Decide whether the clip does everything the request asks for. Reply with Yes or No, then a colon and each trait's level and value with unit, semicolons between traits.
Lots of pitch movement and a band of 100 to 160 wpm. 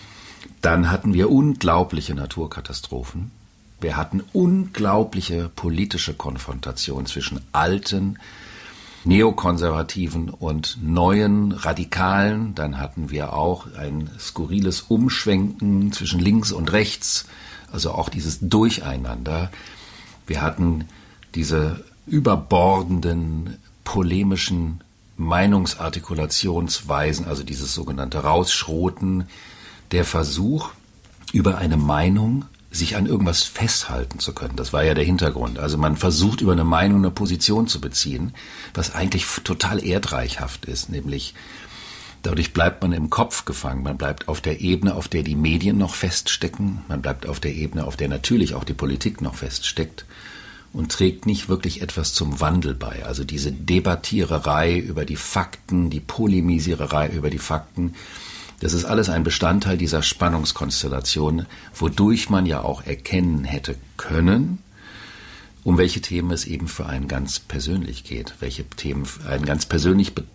No: average, 4.3 semitones; average, 130 wpm